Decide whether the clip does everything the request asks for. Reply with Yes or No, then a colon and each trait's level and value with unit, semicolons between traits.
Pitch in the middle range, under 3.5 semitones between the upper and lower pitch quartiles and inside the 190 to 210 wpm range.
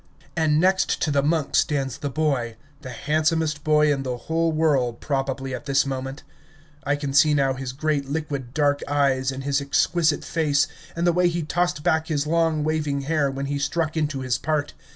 Yes: medium, 145 Hz; narrow, 2.5 semitones; average, 195 wpm